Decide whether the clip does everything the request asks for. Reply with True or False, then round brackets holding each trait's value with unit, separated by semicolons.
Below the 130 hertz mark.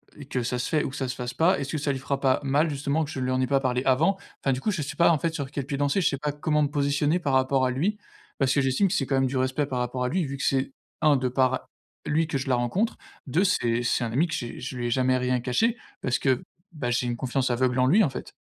False (135 Hz)